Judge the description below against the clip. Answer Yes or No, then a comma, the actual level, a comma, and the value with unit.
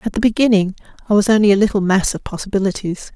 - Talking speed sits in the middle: No, fast, 210 wpm